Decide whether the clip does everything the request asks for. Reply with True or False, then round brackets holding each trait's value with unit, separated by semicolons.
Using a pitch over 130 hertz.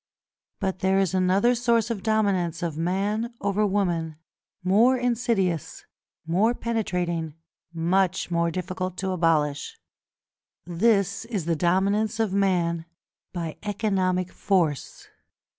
True (190 Hz)